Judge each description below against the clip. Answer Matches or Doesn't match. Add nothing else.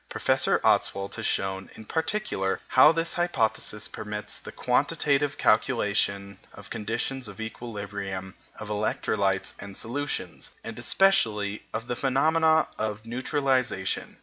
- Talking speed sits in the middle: Doesn't match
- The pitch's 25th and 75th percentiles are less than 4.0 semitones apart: Doesn't match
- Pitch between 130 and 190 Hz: Doesn't match